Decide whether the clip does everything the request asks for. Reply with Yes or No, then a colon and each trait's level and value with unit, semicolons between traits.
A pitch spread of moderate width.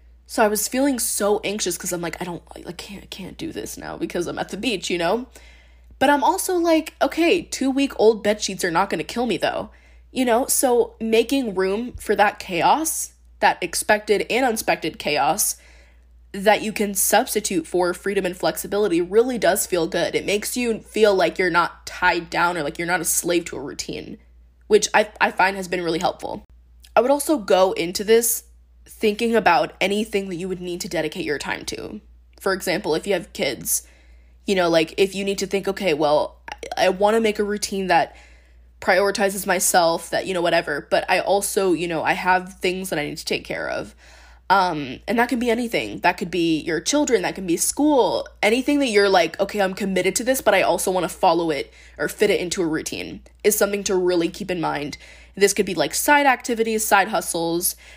Yes: average, 4.6 semitones